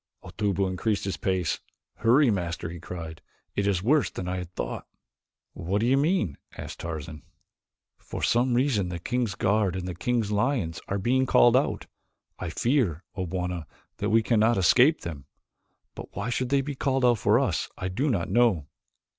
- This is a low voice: Yes, low, 100 Hz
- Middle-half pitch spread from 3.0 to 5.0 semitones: No, wide, 5.5 semitones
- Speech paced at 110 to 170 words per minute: No, average, 180 wpm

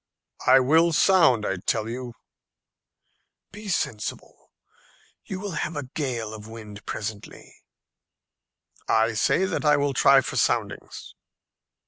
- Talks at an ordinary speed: No, slow, 120 wpm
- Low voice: Yes, low, 130 Hz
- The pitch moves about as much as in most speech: No, wide, 6.1 semitones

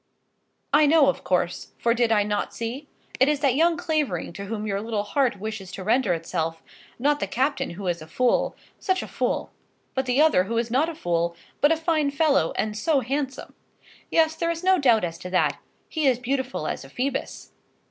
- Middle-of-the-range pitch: No, very high, 250 Hz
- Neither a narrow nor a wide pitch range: No, wide, 6.4 semitones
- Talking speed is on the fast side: Yes, fast, 210 wpm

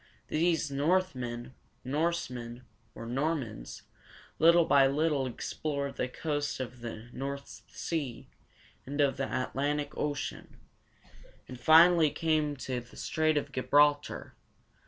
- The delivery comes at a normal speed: No, slow, 115 wpm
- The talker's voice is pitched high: No, medium, 145 Hz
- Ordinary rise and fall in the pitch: Yes, average, 3.4 semitones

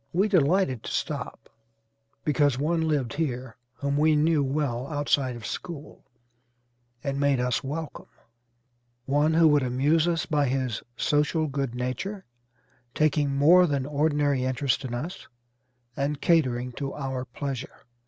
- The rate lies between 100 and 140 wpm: Yes, slow, 135 wpm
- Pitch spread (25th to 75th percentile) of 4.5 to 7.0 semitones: No, average, 3.0 semitones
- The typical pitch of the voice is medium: Yes, medium, 145 Hz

